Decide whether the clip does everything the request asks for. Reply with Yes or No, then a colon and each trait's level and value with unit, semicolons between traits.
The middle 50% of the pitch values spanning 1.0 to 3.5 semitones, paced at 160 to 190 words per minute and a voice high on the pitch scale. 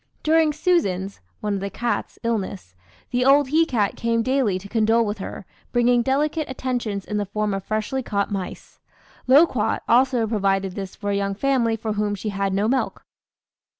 No: average, 4.5 semitones; average, 180 wpm; high, 220 Hz